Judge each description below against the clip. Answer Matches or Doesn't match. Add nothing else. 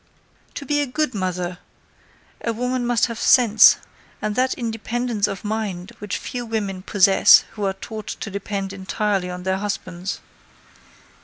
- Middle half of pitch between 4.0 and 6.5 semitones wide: Doesn't match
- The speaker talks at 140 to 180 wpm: Matches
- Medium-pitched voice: Doesn't match